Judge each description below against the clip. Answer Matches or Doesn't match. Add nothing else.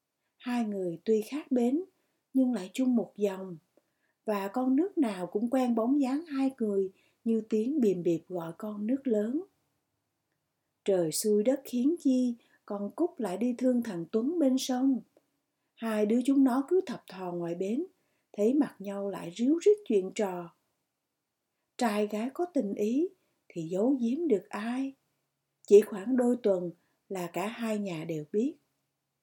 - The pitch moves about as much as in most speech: Matches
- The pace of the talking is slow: Matches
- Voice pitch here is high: Matches